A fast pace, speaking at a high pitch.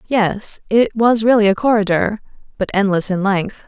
No: average, 165 wpm; high, 210 Hz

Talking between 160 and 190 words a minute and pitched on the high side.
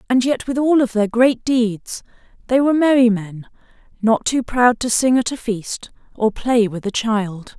No: average, 200 wpm; high, 235 Hz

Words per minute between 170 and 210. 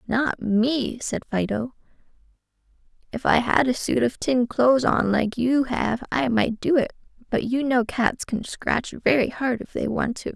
Yes: average, 185 wpm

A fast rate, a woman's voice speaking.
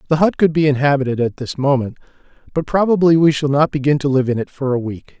No: fast, 240 wpm; male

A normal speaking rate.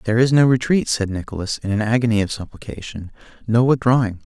Yes: average, 180 wpm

